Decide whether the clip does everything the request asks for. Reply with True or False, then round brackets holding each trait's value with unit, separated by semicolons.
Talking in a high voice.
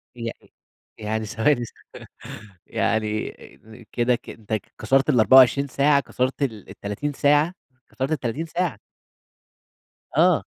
False (125 Hz)